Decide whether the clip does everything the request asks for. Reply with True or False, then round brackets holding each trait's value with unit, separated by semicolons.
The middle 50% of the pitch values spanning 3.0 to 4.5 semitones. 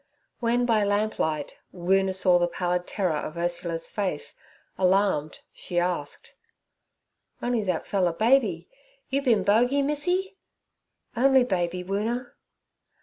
False (5.6 semitones)